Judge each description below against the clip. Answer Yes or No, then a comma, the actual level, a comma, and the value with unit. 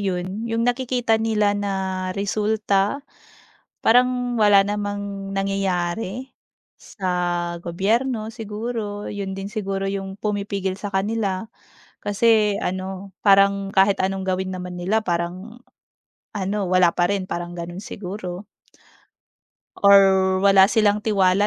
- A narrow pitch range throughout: Yes, narrow, 2.0 semitones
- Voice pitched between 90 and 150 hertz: No, high, 200 Hz